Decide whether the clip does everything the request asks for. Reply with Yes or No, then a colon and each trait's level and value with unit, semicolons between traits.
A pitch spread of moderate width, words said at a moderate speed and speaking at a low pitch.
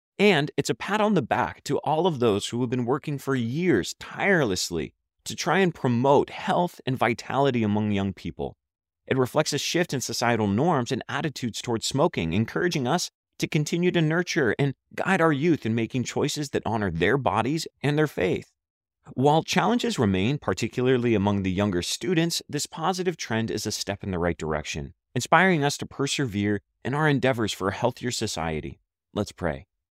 No: wide, 6.8 semitones; average, 180 wpm; low, 125 Hz